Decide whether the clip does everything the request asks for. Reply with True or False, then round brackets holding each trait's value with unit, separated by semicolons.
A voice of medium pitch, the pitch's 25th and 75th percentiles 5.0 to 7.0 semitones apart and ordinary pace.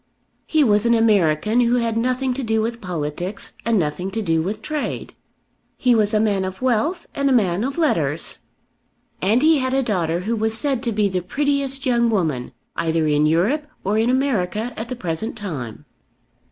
False (220 Hz; 5.6 semitones; 190 wpm)